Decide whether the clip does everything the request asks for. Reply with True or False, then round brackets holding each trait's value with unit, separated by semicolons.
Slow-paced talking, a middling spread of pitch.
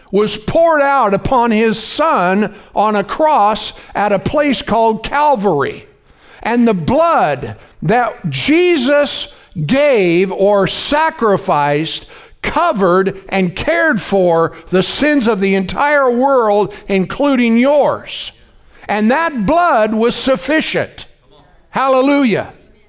False (105 wpm; 6.7 semitones)